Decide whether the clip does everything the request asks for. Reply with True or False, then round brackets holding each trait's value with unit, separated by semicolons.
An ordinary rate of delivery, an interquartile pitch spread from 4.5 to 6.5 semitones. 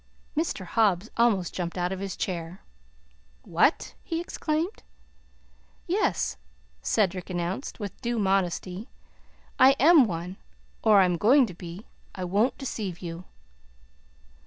False (125 wpm; 5.1 semitones)